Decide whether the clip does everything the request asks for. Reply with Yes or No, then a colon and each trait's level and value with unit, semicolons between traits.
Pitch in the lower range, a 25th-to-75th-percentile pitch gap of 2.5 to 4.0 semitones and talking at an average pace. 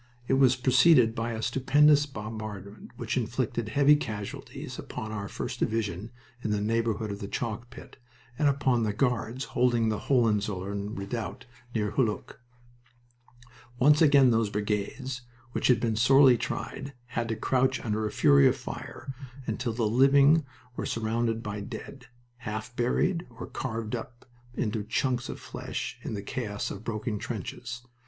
Yes: low, 115 Hz; average, 3.3 semitones; average, 150 wpm